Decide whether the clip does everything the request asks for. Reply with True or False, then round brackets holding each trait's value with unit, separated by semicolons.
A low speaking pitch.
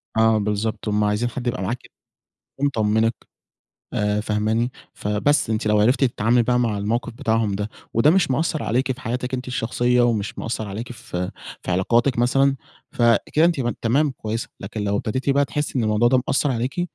True (115 Hz)